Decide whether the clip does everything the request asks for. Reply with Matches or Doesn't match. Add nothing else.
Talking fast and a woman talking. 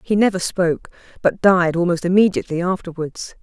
Doesn't match